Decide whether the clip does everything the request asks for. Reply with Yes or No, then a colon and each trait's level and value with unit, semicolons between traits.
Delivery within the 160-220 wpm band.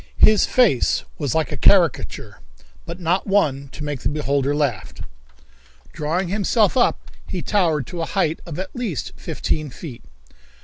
No: average, 150 wpm